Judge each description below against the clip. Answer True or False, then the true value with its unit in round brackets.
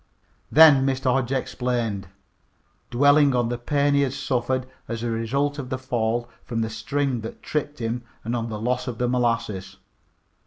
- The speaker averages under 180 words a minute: True (170 wpm)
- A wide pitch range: False (2.9 semitones)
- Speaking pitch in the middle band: False (125 Hz)